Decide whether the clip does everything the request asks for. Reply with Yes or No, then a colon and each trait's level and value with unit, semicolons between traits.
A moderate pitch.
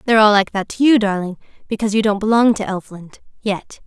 No: high, 210 Hz